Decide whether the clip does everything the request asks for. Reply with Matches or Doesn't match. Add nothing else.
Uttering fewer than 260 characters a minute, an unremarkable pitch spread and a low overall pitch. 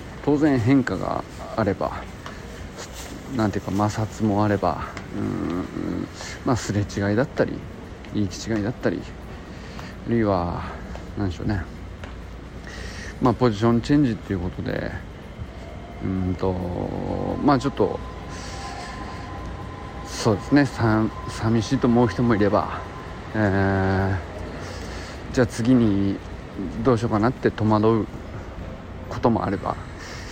Matches